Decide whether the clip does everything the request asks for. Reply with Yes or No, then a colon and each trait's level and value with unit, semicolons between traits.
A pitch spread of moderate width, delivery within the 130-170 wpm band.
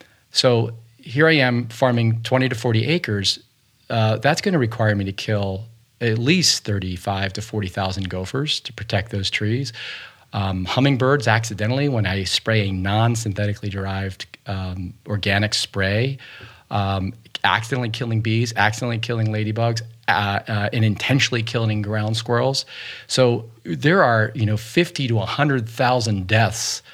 Yes: average, 3.1 semitones; average, 140 wpm